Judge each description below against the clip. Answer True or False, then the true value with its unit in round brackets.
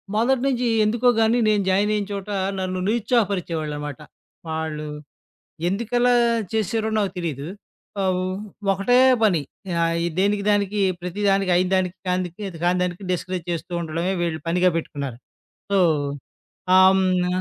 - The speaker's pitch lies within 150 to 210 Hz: True (190 Hz)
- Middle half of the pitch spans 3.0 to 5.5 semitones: True (3.3 semitones)